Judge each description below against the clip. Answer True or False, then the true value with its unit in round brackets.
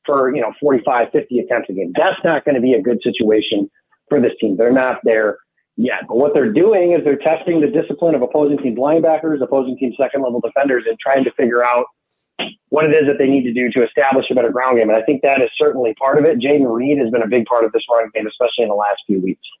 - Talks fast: True (255 wpm)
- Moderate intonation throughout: True (4.3 semitones)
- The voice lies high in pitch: False (135 Hz)